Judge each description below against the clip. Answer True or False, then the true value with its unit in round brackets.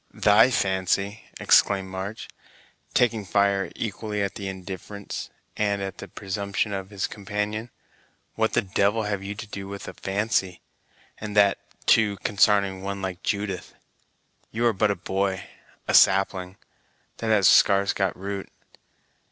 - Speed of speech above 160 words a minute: False (145 wpm)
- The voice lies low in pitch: True (100 Hz)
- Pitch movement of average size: False (1.3 semitones)